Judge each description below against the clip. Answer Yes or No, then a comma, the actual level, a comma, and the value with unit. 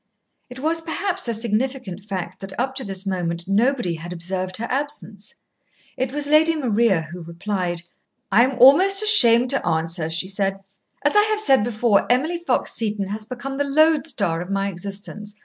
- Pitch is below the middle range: No, high, 215 Hz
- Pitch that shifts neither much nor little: No, wide, 6.5 semitones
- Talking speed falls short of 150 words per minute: No, average, 175 wpm